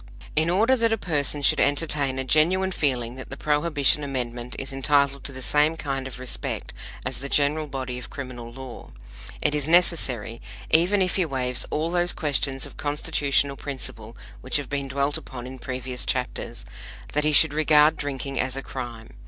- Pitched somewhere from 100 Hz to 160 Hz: Yes, medium, 140 Hz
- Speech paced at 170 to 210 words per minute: Yes, average, 180 wpm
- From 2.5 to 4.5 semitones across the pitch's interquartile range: Yes, average, 2.9 semitones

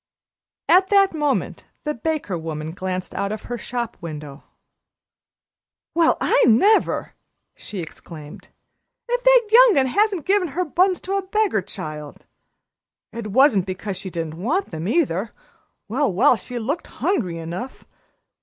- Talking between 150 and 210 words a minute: No, slow, 135 wpm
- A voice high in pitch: Yes, high, 235 Hz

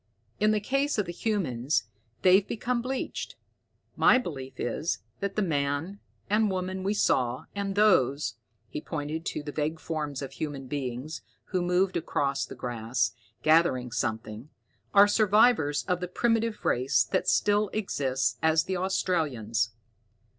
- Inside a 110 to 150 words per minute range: Yes, average, 145 wpm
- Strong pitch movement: Yes, wide, 6.8 semitones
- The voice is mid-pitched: Yes, medium, 160 Hz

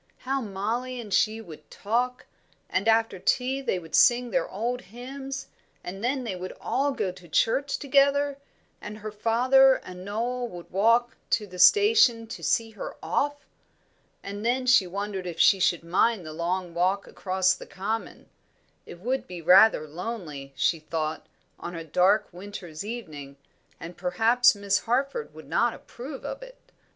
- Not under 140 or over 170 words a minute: Yes, average, 165 wpm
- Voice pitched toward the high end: Yes, high, 215 Hz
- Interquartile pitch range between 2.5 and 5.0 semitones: No, wide, 5.4 semitones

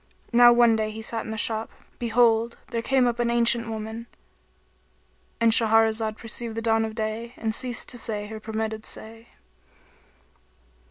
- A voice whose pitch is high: Yes, high, 225 Hz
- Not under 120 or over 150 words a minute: No, average, 160 wpm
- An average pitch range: No, narrow, 1.3 semitones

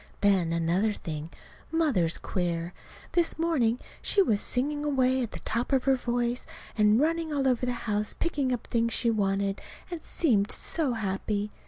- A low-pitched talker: No, high, 235 Hz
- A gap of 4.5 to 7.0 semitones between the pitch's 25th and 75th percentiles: Yes, wide, 5.4 semitones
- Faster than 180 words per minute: No, average, 165 wpm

